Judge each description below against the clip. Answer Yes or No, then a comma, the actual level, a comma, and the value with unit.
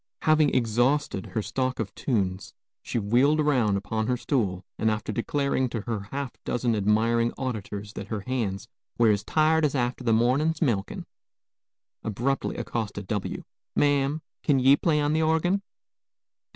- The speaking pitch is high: No, low, 120 Hz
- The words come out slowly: No, average, 150 wpm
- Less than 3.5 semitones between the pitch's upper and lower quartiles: No, average, 4.8 semitones